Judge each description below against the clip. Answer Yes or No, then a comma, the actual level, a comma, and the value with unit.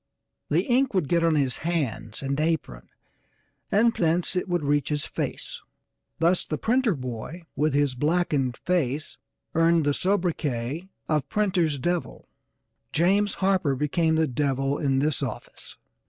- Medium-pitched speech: Yes, medium, 155 Hz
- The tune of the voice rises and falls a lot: No, average, 4.2 semitones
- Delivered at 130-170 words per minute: Yes, average, 140 wpm